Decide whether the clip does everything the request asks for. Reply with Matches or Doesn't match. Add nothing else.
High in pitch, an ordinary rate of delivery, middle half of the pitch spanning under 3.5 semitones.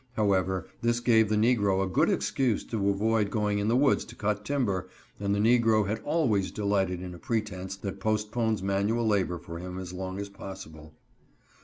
Doesn't match